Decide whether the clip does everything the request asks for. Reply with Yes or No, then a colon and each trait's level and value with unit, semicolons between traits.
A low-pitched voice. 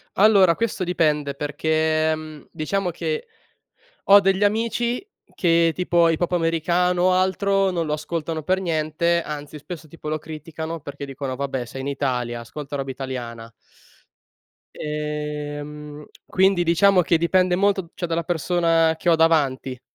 No: medium, 160 Hz